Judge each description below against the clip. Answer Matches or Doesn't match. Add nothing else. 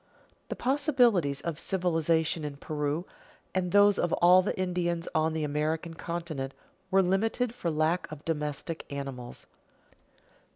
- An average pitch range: Matches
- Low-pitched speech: Doesn't match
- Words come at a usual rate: Doesn't match